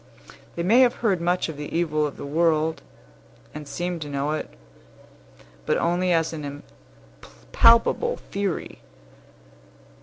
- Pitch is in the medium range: Yes, medium, 165 Hz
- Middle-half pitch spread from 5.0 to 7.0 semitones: No, average, 3.3 semitones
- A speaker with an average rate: No, slow, 130 wpm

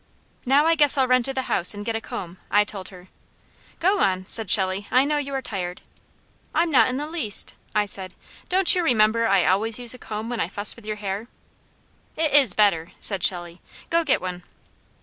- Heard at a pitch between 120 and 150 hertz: No, high, 215 Hz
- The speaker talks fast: Yes, fast, 210 wpm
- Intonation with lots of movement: Yes, wide, 5.9 semitones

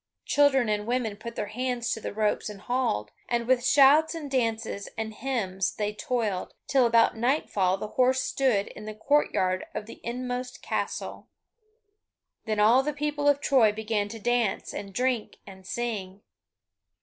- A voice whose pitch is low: No, high, 230 Hz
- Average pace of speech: Yes, average, 160 wpm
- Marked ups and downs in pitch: No, average, 3.7 semitones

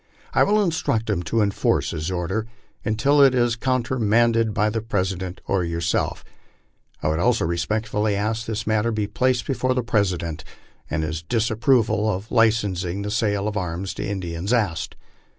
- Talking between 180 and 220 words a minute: No, average, 170 wpm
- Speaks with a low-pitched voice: Yes, low, 105 Hz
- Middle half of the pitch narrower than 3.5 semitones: No, average, 3.9 semitones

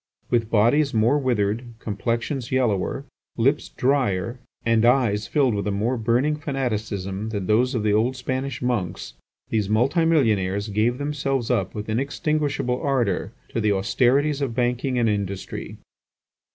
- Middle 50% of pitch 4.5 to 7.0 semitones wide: No, average, 4.1 semitones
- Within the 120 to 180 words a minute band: Yes, average, 140 wpm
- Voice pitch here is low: Yes, low, 120 Hz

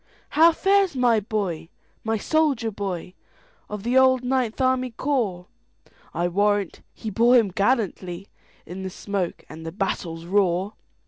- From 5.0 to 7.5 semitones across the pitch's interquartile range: Yes, wide, 5.6 semitones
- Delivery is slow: Yes, slow, 120 wpm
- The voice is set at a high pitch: Yes, high, 210 Hz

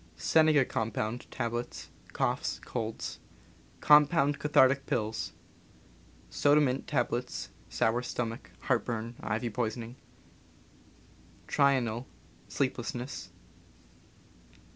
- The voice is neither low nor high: No, low, 125 Hz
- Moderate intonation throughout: Yes, average, 3.4 semitones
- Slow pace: Yes, slow, 85 wpm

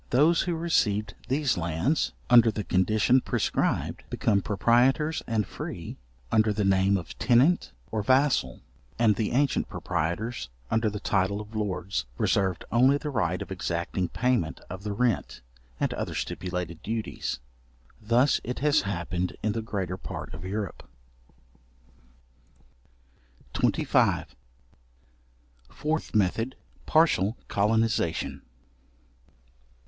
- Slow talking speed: Yes, slow, 115 wpm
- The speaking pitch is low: Yes, low, 110 Hz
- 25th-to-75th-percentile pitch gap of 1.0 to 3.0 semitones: No, average, 4.8 semitones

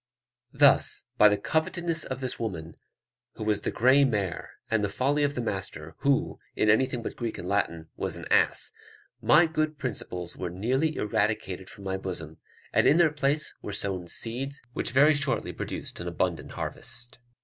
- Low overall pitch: Yes, low, 115 Hz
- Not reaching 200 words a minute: Yes, average, 175 wpm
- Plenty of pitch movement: Yes, wide, 6.2 semitones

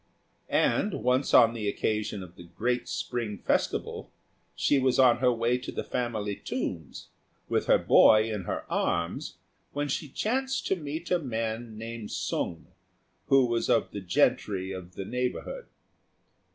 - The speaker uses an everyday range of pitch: Yes, average, 4.1 semitones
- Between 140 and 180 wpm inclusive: Yes, average, 155 wpm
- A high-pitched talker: No, low, 115 Hz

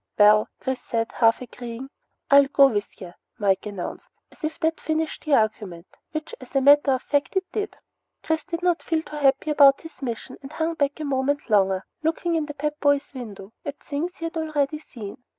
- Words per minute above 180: Yes, fast, 205 wpm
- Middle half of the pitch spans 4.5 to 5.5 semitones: Yes, average, 5.1 semitones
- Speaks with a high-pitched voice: Yes, very high, 280 Hz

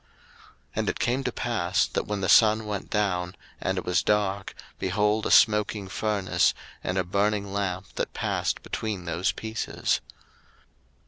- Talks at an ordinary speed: Yes, average, 155 wpm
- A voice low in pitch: Yes, low, 100 Hz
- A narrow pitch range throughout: Yes, narrow, 2.2 semitones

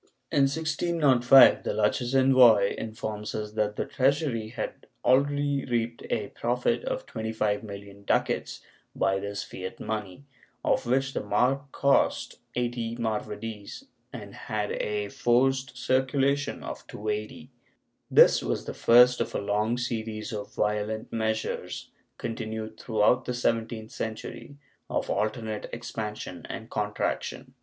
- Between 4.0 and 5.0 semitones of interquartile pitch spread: No, average, 3.5 semitones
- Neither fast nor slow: No, slow, 125 wpm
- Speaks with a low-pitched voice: Yes, low, 115 Hz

